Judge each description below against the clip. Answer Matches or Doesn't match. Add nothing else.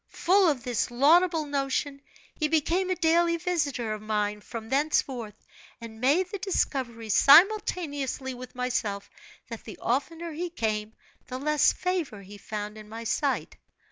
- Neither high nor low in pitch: Doesn't match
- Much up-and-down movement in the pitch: Matches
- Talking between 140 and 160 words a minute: Matches